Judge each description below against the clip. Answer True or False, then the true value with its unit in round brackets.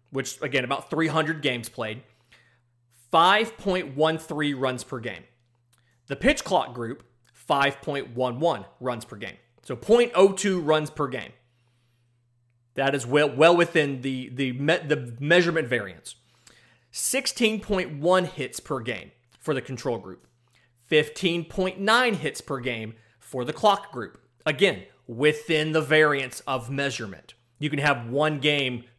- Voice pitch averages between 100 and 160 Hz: True (135 Hz)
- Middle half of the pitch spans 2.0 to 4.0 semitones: False (4.6 semitones)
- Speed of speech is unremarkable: False (125 wpm)